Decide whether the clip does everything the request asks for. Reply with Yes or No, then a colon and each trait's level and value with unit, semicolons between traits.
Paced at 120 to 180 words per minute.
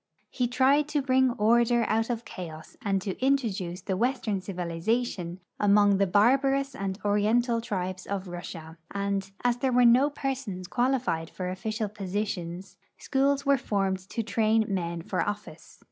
Yes: average, 145 wpm